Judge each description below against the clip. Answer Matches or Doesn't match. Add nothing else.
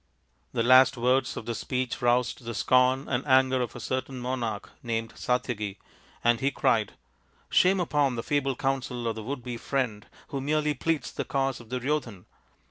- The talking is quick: Doesn't match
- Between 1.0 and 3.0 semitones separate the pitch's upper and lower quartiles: Matches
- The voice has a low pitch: Matches